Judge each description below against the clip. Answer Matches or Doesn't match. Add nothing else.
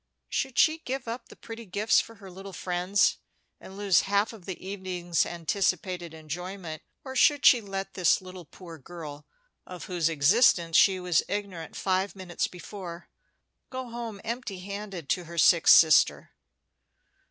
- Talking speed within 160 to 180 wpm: Doesn't match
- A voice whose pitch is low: Doesn't match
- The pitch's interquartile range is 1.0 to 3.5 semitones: Matches